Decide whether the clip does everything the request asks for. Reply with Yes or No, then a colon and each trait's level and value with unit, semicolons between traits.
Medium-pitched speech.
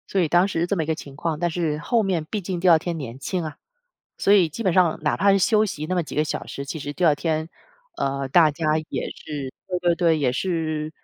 Yes: medium, 165 Hz